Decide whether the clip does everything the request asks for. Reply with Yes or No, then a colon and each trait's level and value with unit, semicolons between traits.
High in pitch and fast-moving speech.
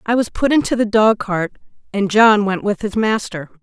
Yes: high, 210 Hz; fast, 215 wpm